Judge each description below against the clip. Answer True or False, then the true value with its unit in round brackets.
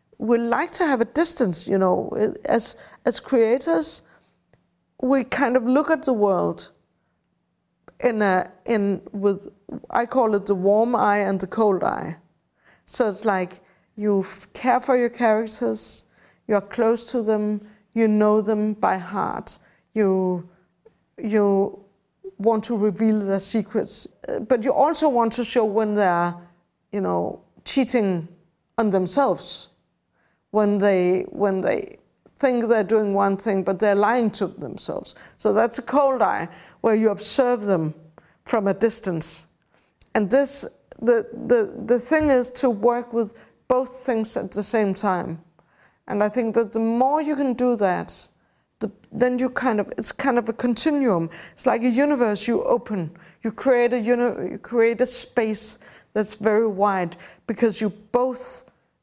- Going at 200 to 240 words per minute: False (155 wpm)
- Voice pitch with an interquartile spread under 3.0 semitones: False (3.9 semitones)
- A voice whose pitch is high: True (220 Hz)